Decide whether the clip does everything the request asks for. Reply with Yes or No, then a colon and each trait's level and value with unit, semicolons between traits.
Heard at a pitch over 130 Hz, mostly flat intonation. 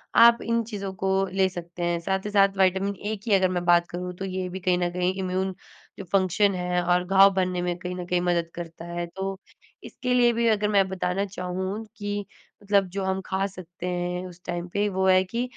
Yes: high, 190 Hz; narrow, 1.7 semitones